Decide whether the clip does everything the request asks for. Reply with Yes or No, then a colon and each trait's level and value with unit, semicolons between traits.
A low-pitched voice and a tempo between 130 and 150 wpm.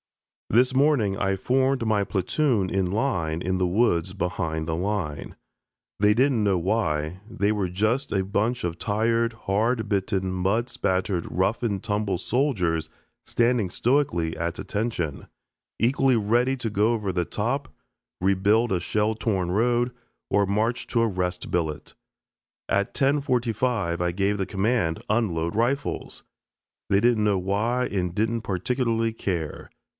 Yes: low, 105 Hz; average, 140 wpm